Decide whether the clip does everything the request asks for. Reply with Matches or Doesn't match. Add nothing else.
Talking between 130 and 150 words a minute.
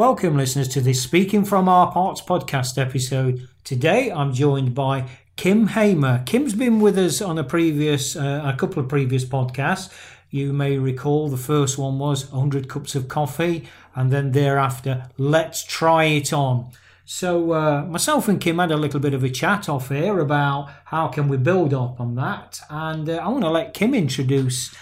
Doesn't match